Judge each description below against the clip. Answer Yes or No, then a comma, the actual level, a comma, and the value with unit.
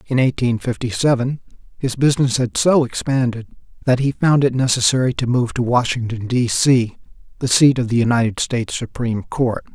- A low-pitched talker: Yes, low, 125 Hz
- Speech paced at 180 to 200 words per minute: No, average, 170 wpm